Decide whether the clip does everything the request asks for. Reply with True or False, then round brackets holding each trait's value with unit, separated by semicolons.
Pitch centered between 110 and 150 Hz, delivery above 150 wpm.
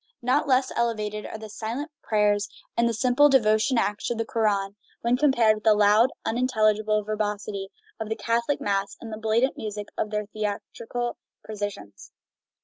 False (215 Hz; 160 wpm)